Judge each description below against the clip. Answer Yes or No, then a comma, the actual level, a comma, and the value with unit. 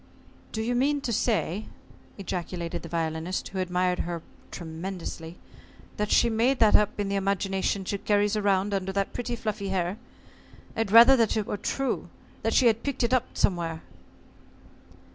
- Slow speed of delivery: No, average, 160 wpm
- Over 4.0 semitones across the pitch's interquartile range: No, average, 3.6 semitones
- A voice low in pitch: No, high, 200 Hz